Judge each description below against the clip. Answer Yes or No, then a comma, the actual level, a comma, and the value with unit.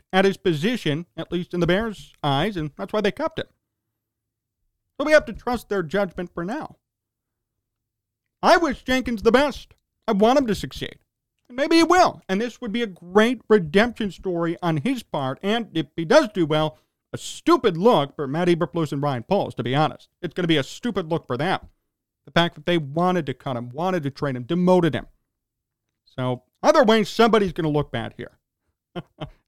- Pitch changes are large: Yes, wide, 7.7 semitones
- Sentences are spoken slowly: No, average, 200 wpm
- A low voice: No, medium, 175 Hz